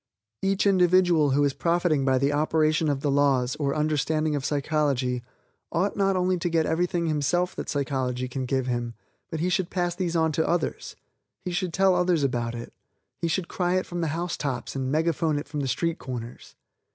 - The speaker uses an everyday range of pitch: Yes, average, 4.1 semitones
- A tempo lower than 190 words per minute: No, average, 195 wpm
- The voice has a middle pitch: Yes, medium, 155 Hz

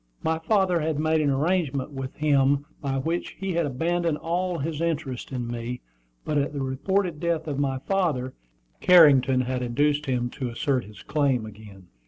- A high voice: No, medium, 145 Hz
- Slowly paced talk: No, average, 175 wpm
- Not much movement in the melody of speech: No, average, 3.9 semitones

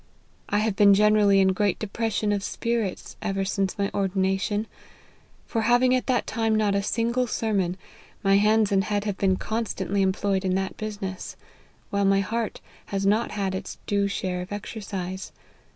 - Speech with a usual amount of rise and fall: No, narrow, 2.0 semitones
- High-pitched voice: Yes, high, 200 Hz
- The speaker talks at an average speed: Yes, average, 170 wpm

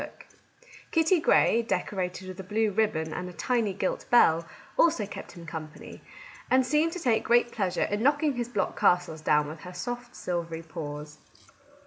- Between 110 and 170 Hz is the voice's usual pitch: No, high, 195 Hz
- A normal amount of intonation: No, wide, 6.6 semitones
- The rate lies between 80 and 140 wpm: No, average, 165 wpm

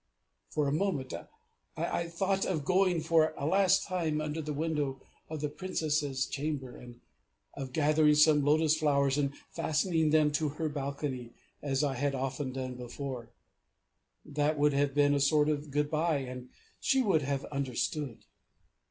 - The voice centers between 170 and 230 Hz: No, medium, 150 Hz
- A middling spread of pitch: No, narrow, 2.3 semitones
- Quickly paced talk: No, average, 160 wpm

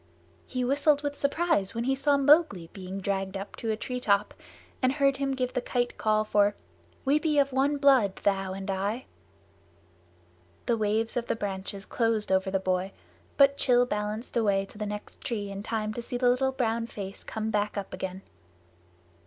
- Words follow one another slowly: No, average, 180 wpm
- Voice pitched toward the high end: Yes, high, 220 Hz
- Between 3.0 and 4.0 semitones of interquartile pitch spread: No, average, 5.0 semitones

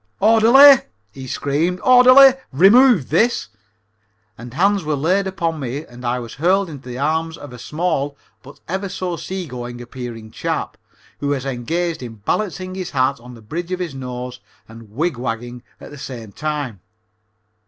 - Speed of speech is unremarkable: Yes, average, 165 wpm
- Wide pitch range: Yes, wide, 6.9 semitones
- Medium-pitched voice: Yes, medium, 145 Hz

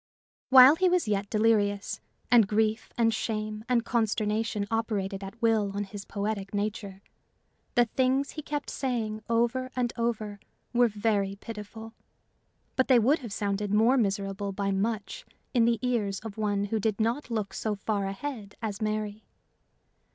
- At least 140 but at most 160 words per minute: Yes, average, 155 wpm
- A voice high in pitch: Yes, high, 215 Hz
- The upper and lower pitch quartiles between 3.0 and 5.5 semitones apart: No, narrow, 2.6 semitones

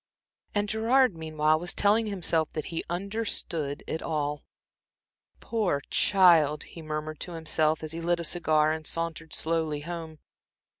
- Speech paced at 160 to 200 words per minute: No, average, 145 wpm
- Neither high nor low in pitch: Yes, medium, 165 Hz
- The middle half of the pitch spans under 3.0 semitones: Yes, narrow, 2.4 semitones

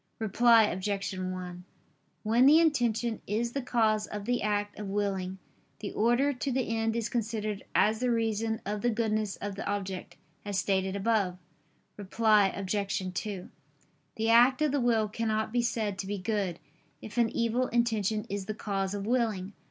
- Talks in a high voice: Yes, high, 215 Hz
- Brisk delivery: No, average, 170 wpm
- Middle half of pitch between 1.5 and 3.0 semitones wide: Yes, average, 2.7 semitones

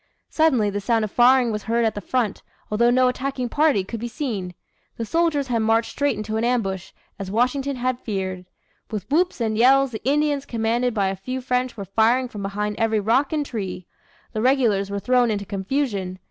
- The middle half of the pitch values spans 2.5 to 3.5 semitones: No, average, 3.9 semitones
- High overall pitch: Yes, high, 230 Hz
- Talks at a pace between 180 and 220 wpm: Yes, average, 200 wpm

